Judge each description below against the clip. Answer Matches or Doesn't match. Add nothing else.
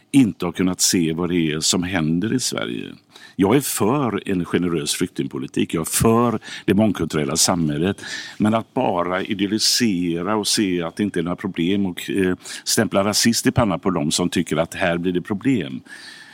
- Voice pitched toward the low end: Matches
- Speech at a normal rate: Matches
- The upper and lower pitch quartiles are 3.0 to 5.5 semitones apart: Matches